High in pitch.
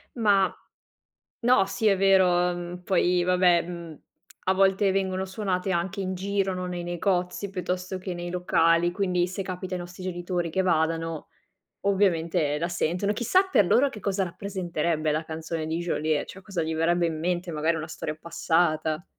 No: medium, 180 Hz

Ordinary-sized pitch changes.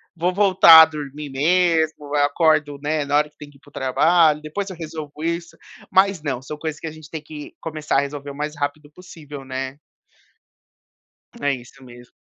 No: narrow, 2.2 semitones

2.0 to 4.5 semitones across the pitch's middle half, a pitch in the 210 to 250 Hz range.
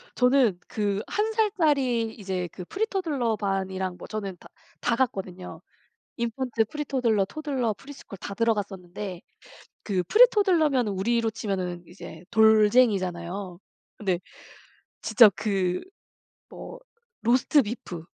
No: average, 5.3 semitones; high, 220 Hz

